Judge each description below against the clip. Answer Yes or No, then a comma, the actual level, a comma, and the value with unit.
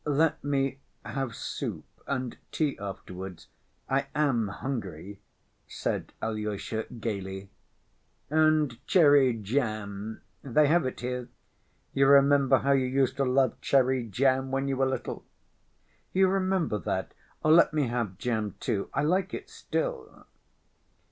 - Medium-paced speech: No, slow, 130 wpm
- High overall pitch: No, low, 130 Hz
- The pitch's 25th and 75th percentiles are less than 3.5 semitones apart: No, average, 4.8 semitones